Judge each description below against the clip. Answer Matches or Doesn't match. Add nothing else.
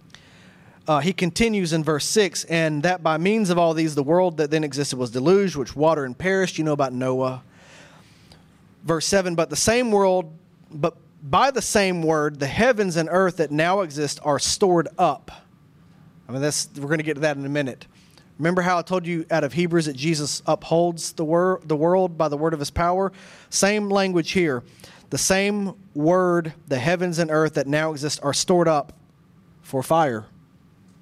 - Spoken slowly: Doesn't match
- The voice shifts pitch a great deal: Doesn't match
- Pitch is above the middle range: Doesn't match